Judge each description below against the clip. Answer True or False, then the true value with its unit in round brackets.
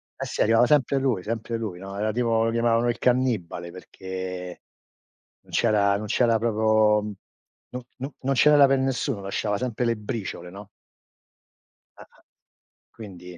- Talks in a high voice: False (110 Hz)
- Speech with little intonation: False (3.6 semitones)